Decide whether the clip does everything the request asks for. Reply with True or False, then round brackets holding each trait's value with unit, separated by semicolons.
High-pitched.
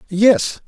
True (215 Hz)